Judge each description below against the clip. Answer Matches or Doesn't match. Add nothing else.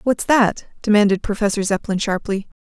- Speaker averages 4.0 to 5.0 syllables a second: Doesn't match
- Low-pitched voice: Doesn't match